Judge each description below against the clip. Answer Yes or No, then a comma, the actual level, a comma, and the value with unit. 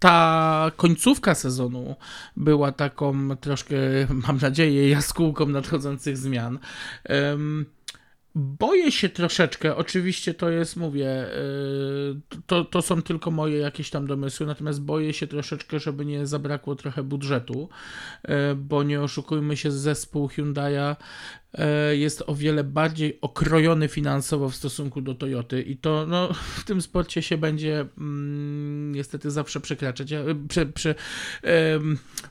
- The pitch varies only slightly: Yes, narrow, 1.9 semitones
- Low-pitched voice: No, medium, 150 Hz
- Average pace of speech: Yes, average, 130 wpm